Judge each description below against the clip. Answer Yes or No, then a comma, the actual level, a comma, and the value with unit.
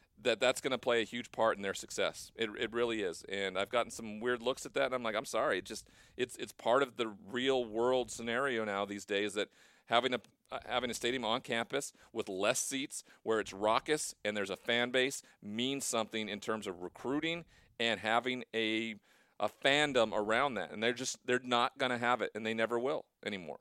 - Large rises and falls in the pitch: No, narrow, 2.5 semitones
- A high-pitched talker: No, low, 115 Hz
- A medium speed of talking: No, fast, 225 wpm